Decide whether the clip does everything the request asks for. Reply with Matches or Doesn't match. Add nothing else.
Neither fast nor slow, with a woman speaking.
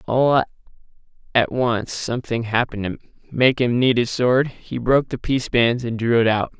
Doesn't match